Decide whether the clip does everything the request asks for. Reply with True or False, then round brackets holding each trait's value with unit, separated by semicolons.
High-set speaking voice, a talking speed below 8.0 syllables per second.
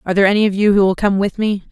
False (200 Hz; 8.4 syllables/s)